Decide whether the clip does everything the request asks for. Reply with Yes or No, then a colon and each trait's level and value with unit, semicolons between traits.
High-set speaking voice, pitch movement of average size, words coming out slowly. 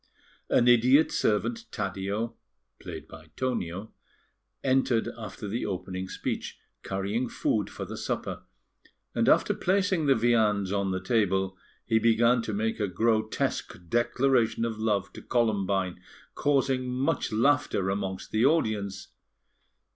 No: low, 110 Hz; average, 4.0 semitones; slow, 125 wpm